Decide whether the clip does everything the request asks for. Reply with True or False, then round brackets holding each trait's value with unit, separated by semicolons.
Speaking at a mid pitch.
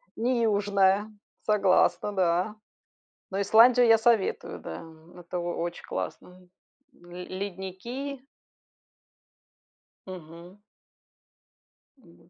False (195 Hz)